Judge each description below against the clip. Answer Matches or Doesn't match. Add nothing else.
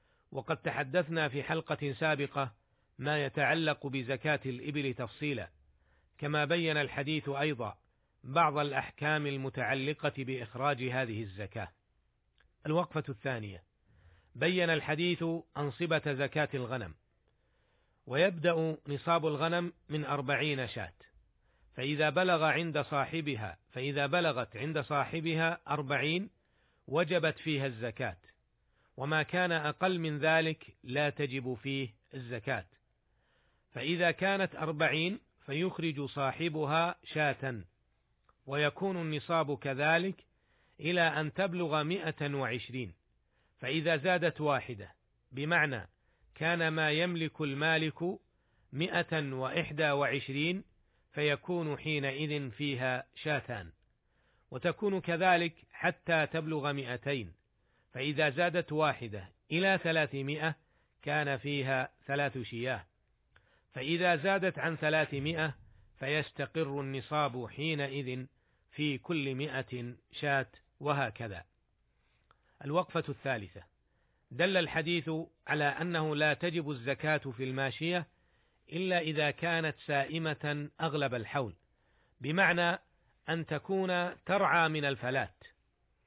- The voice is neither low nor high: Matches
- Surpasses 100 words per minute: Doesn't match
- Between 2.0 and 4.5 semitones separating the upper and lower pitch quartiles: Matches